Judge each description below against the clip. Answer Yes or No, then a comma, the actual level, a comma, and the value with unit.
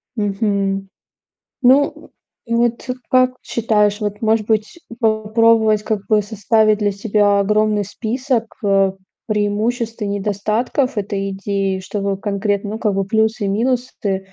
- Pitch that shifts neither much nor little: No, narrow, 2.1 semitones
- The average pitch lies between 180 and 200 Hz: No, high, 210 Hz